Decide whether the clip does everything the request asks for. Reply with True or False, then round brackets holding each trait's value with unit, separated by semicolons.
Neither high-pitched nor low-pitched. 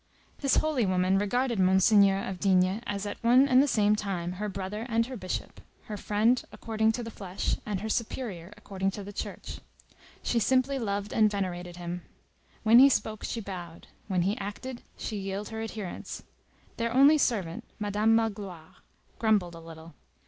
False (205 Hz)